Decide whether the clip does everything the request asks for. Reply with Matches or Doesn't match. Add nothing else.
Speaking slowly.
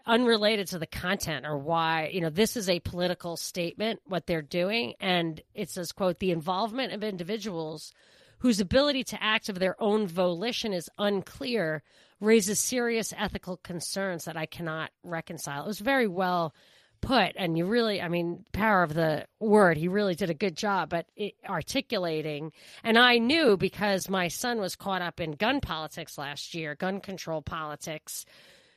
Doesn't match